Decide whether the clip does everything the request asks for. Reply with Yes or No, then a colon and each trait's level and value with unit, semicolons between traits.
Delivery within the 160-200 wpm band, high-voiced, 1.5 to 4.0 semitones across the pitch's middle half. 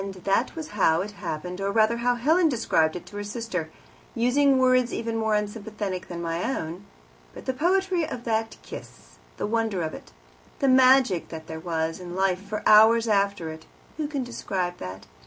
No: average, 185 wpm; high, 210 Hz; wide, 5.6 semitones